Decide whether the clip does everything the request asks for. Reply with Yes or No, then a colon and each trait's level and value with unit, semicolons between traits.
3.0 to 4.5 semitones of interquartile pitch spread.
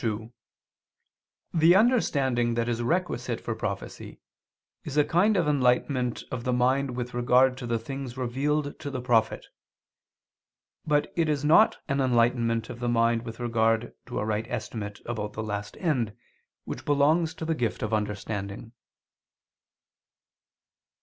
Yes: average, 3.9 semitones